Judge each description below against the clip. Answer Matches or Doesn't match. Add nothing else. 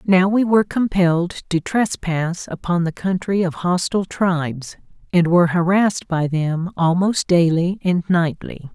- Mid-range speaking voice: Matches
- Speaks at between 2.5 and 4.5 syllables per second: Matches